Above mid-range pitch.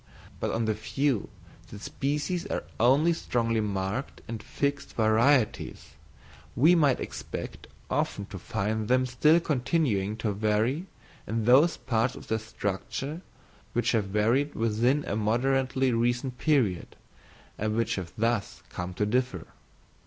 No: low, 115 Hz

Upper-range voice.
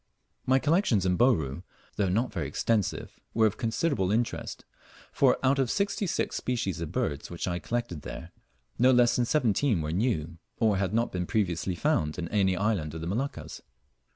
No: low, 105 Hz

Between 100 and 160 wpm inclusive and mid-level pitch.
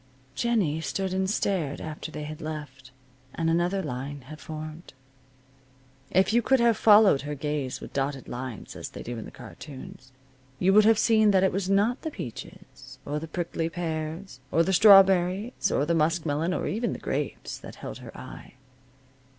No: average, 175 wpm; medium, 165 Hz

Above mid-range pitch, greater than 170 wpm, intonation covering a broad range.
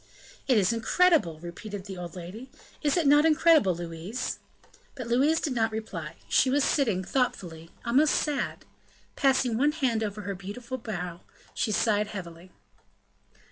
No: high, 220 Hz; average, 145 wpm; wide, 6.7 semitones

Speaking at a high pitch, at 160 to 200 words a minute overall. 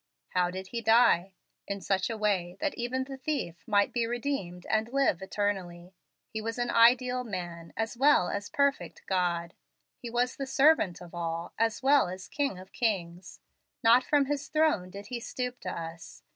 Yes: high, 220 Hz; average, 180 wpm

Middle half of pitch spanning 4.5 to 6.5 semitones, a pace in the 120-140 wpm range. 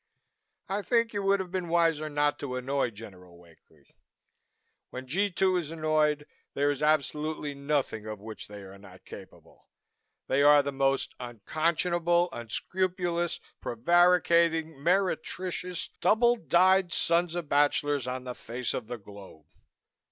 Yes: wide, 5.5 semitones; slow, 135 wpm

